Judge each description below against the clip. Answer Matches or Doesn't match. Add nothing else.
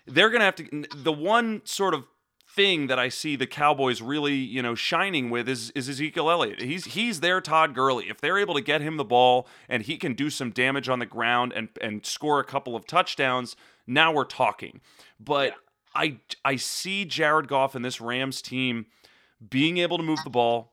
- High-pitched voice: Doesn't match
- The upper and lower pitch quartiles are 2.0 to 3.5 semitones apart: Doesn't match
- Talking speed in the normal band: Doesn't match